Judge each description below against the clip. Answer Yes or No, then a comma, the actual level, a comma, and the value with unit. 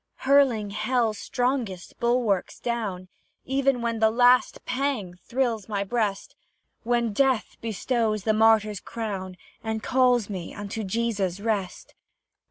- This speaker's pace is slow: Yes, slow, 120 wpm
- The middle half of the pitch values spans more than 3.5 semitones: No, average, 3.2 semitones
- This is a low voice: No, high, 225 Hz